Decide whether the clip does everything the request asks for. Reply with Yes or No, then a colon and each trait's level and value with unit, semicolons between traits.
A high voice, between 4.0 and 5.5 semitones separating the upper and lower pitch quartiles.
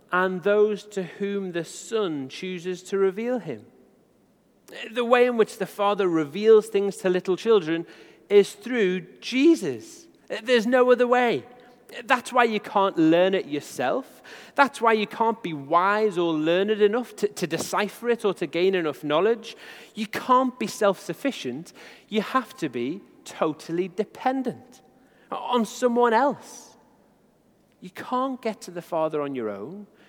Yes: high, 205 Hz; average, 4.9 semitones